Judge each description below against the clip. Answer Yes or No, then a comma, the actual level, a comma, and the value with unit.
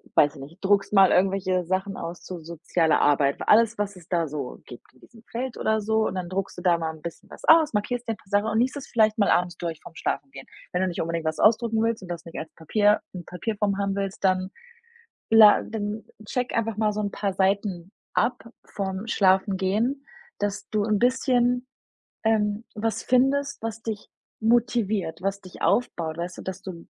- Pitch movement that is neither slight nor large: Yes, average, 3.9 semitones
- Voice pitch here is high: Yes, high, 200 Hz